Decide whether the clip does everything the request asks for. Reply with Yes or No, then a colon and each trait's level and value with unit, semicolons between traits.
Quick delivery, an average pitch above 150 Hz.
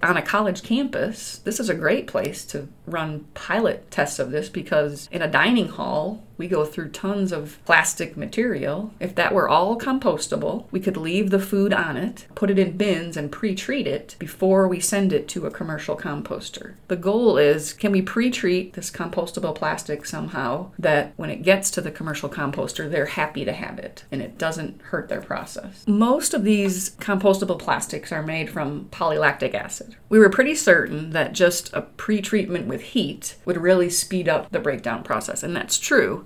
No: average, 185 wpm; high, 190 Hz